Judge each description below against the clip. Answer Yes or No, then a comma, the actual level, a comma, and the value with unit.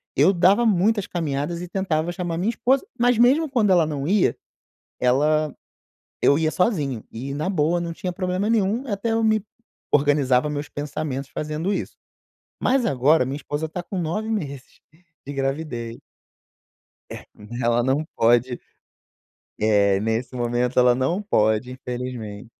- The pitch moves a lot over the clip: Yes, wide, 6.8 semitones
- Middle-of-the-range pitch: Yes, medium, 155 Hz